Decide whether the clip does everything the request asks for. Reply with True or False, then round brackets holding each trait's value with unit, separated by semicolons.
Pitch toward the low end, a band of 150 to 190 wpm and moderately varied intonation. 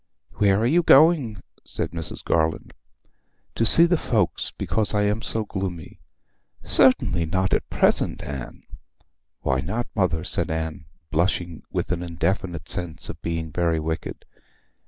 False (90 Hz; 140 wpm; 4.7 semitones)